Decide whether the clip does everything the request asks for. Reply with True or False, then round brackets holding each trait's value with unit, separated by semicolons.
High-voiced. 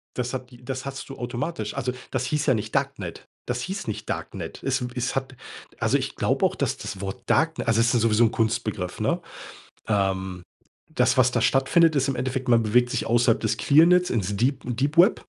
False (125 Hz)